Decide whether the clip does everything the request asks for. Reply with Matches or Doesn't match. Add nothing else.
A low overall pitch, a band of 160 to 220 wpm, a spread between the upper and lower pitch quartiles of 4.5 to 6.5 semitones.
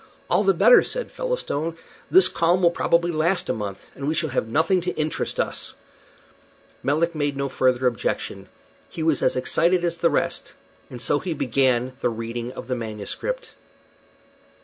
Doesn't match